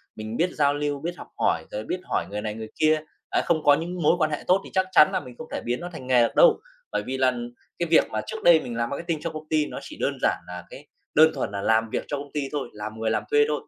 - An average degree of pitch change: No, wide, 5.7 semitones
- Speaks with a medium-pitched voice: Yes, medium, 145 Hz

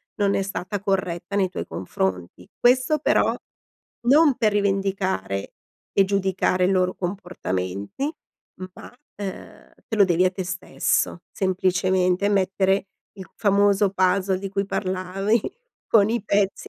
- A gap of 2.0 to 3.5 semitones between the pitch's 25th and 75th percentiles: No, narrow, 1.6 semitones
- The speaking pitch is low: No, high, 190 Hz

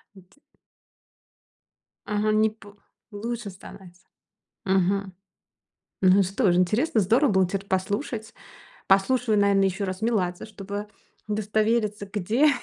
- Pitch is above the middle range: Yes, high, 205 Hz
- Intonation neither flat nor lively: No, narrow, 2.3 semitones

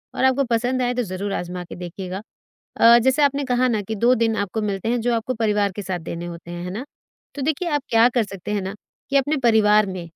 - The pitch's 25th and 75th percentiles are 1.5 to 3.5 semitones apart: No, average, 4.5 semitones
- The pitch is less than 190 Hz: No, high, 220 Hz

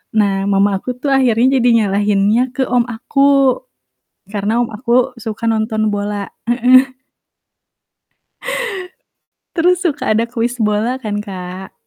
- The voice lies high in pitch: Yes, high, 230 Hz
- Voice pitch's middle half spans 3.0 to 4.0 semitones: Yes, average, 3.6 semitones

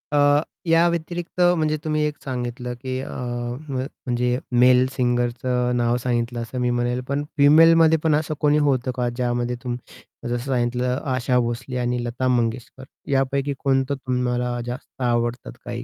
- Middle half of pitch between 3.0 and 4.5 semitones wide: No, narrow, 2.4 semitones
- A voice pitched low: Yes, low, 125 Hz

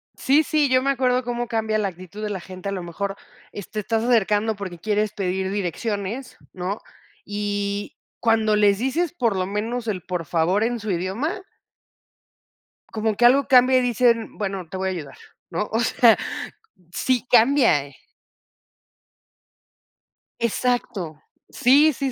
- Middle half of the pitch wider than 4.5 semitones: No, average, 4.2 semitones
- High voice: Yes, high, 215 Hz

